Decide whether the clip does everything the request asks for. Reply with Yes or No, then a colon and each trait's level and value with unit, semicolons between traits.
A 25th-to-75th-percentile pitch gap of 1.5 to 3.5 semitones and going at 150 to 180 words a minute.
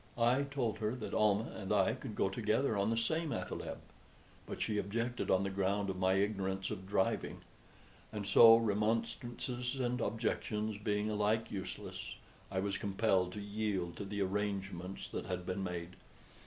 Yes: average, 2.8 semitones; average, 165 wpm